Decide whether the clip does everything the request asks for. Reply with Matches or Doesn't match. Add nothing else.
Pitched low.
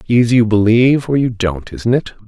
Matches